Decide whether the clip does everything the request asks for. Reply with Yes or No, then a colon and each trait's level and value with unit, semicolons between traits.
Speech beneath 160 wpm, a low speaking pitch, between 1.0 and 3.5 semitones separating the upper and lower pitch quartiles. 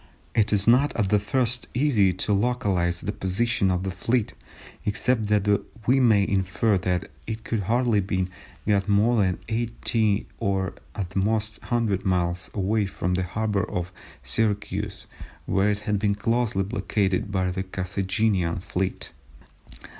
Yes: average, 150 wpm; low, 100 Hz; average, 2.9 semitones